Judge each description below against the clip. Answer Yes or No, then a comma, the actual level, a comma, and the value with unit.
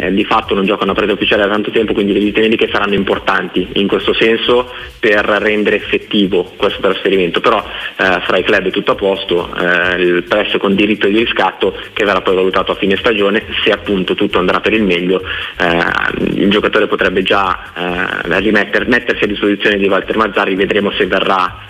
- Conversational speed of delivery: No, fast, 195 wpm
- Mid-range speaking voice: No, low, 100 Hz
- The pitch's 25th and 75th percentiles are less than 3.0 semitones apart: Yes, narrow, 2.6 semitones